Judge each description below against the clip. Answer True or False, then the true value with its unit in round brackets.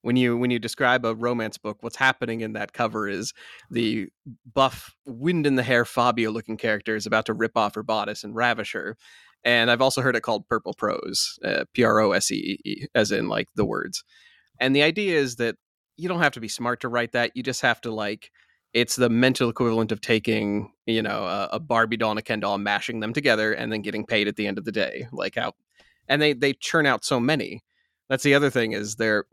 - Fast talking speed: True (235 wpm)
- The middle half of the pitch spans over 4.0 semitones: False (2.8 semitones)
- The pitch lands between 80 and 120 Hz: True (115 Hz)